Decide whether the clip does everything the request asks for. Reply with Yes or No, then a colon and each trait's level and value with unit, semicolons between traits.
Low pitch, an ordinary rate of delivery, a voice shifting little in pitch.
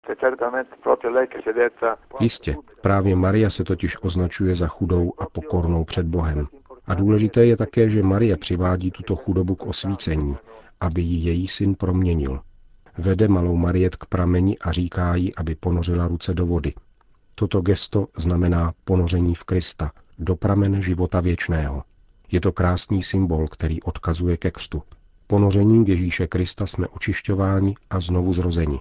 Yes: very low, 90 Hz; average, 140 wpm; narrow, 2.2 semitones